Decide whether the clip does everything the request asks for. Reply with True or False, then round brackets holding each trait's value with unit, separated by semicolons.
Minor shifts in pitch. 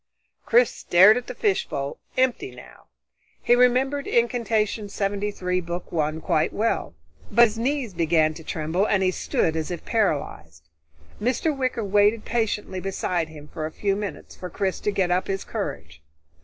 False (5.5 semitones)